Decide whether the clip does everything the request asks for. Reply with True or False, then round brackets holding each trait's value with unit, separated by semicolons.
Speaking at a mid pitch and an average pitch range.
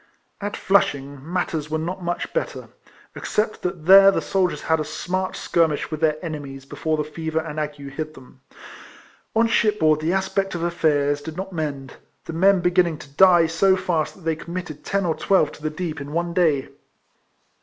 True (160 Hz; 3.3 semitones)